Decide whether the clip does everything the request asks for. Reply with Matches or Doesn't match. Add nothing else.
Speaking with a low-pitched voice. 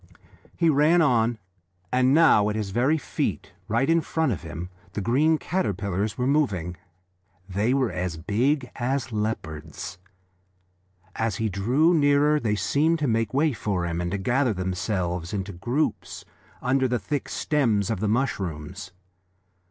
Matches